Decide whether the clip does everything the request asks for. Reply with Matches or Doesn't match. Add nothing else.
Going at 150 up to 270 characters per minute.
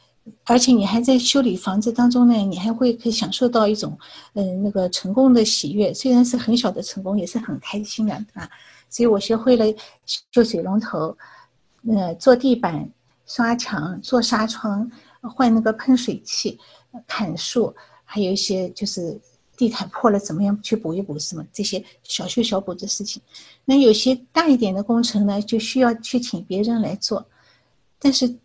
Matches